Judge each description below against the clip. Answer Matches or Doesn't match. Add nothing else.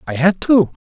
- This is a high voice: Doesn't match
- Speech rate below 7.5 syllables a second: Matches